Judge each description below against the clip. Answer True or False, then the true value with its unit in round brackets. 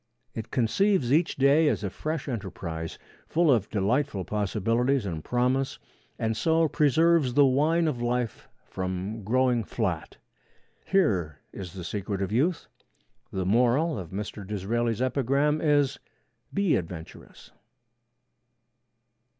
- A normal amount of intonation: False (6.6 semitones)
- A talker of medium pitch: False (120 Hz)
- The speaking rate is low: True (120 wpm)